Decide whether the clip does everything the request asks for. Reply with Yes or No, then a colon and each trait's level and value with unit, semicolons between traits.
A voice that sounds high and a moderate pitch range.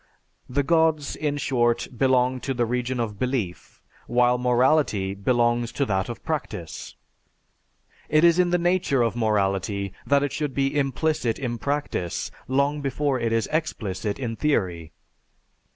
No: low, 125 Hz; average, 4.1 semitones